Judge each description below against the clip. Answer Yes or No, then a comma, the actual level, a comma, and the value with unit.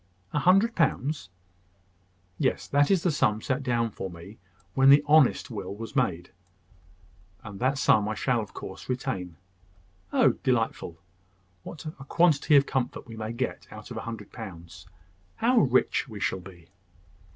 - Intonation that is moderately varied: No, wide, 6.1 semitones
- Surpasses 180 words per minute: No, average, 160 wpm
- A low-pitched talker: Yes, low, 115 Hz